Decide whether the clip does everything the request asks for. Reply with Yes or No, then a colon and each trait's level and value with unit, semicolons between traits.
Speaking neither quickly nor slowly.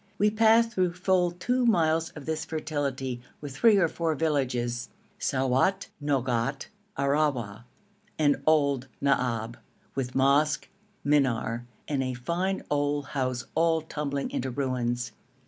No: slow, 125 wpm